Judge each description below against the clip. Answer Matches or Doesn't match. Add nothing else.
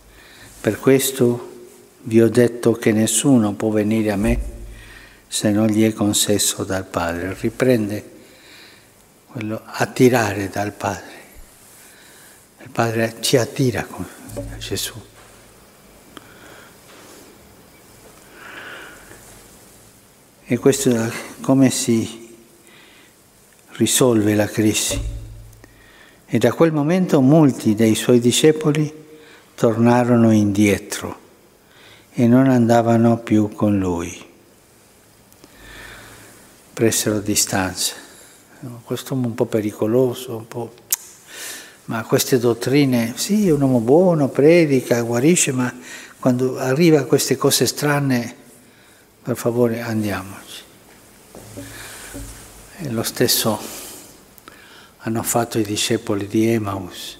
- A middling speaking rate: Doesn't match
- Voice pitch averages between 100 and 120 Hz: Matches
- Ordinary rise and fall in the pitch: Matches